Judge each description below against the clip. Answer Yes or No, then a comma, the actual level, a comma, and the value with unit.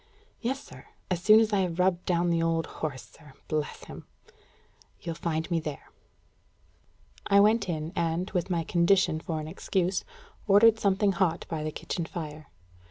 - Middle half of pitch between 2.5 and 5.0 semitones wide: Yes, average, 3.2 semitones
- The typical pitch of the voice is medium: Yes, medium, 170 Hz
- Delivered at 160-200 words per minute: Yes, average, 165 wpm